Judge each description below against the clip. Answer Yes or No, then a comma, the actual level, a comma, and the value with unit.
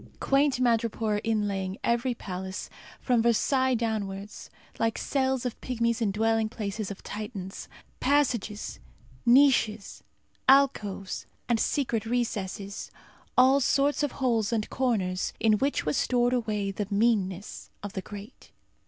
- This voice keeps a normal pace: No, slow, 125 wpm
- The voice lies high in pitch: Yes, high, 225 Hz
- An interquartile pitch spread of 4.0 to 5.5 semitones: No, average, 3.5 semitones